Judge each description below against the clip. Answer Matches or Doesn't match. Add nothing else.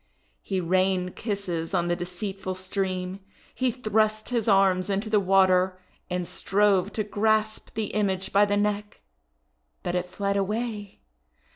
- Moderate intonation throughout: Doesn't match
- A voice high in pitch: Matches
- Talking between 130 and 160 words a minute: Matches